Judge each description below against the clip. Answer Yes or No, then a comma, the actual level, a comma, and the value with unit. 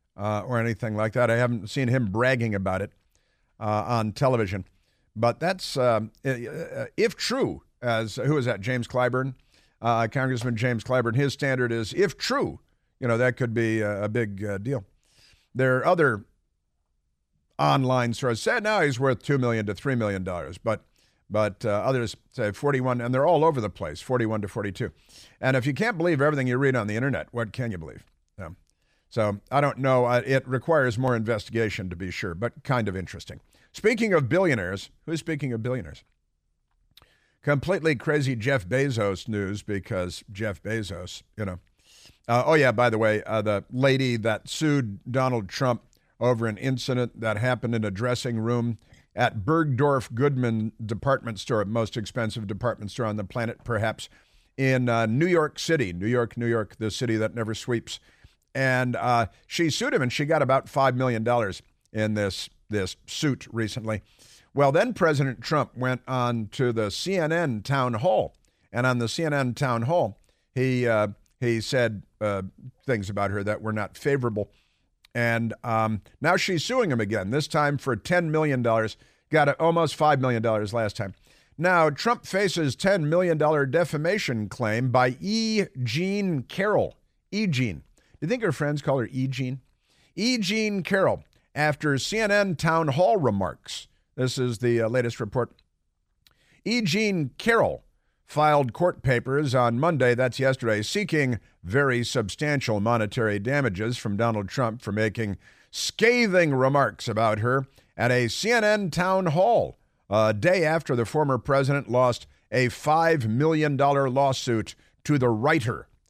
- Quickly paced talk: No, average, 165 wpm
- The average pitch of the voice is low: Yes, low, 125 Hz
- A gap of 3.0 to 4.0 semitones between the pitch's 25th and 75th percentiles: No, average, 4.4 semitones